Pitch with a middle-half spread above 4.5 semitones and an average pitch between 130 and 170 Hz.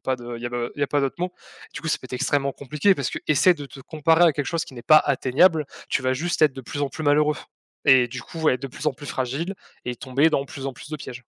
No: average, 3.0 semitones; medium, 140 Hz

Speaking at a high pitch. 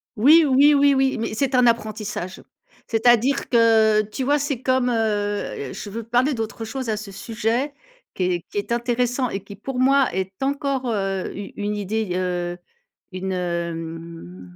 Yes: high, 225 Hz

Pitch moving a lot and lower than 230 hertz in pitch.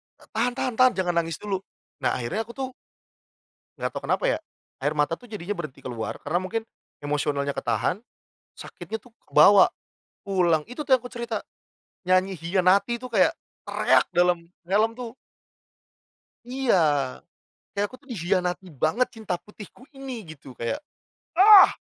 Yes: wide, 6.3 semitones; high, 190 Hz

